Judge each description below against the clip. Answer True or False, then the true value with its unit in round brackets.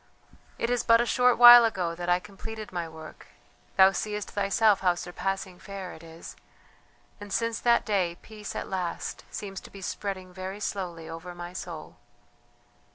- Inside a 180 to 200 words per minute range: False (165 wpm)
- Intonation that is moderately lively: True (3.2 semitones)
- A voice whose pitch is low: False (195 Hz)